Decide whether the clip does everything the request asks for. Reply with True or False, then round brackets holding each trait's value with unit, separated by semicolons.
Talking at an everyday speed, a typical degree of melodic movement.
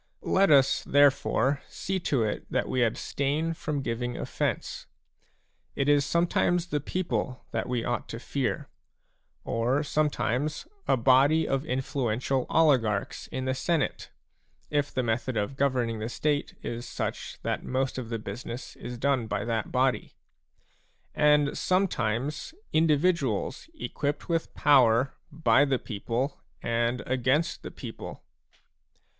False (130 wpm; 3.7 semitones)